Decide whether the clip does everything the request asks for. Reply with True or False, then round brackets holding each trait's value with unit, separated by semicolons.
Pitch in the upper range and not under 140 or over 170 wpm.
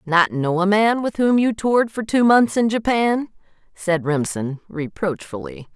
True (200 Hz; 165 wpm)